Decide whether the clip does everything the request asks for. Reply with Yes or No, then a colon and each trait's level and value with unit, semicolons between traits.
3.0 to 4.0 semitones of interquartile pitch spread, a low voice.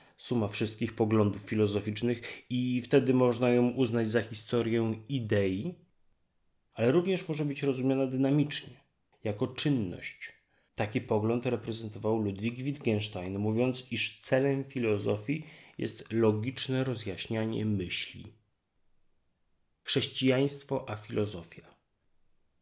Yes: average, 3.6 semitones; low, 115 Hz